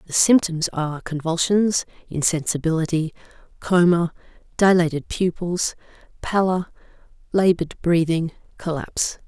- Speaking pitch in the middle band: Yes, medium, 170 Hz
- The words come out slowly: Yes, slow, 80 wpm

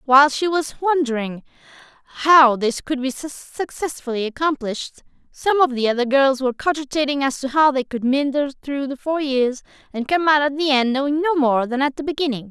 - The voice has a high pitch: Yes, very high, 275 Hz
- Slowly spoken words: No, average, 190 wpm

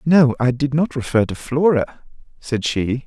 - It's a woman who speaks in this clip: No, male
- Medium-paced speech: Yes, average, 175 wpm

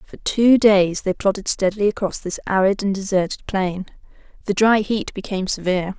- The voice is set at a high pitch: Yes, high, 195 Hz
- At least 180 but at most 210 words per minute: No, average, 170 wpm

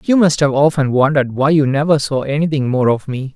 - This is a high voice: No, medium, 140 Hz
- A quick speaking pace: Yes, fast, 235 wpm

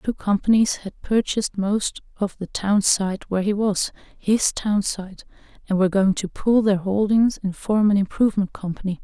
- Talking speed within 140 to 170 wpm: Yes, average, 165 wpm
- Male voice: No, female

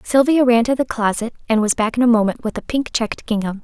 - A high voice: Yes, high, 230 Hz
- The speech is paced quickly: Yes, fast, 265 wpm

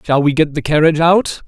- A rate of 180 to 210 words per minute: No, fast, 245 wpm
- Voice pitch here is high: No, medium, 155 Hz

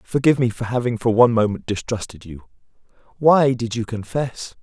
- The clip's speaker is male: Yes, male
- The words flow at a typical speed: Yes, average, 170 wpm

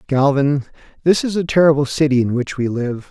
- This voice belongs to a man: Yes, male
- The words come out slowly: No, average, 195 wpm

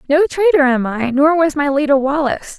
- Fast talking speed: Yes, fast, 210 wpm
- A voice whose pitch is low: No, very high, 290 Hz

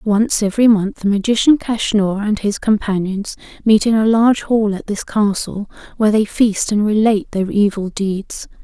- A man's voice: No, female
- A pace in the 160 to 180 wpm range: Yes, average, 175 wpm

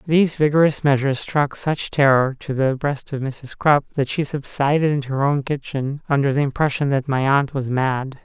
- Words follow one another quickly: No, average, 195 wpm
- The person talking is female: No, male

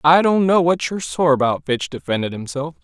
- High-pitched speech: No, medium, 150 Hz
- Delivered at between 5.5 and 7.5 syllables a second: Yes, 5.6 syllables/s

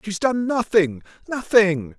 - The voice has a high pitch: Yes, high, 200 Hz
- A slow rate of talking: Yes, slow, 120 wpm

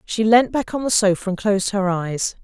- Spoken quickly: Yes, fast, 245 wpm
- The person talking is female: Yes, female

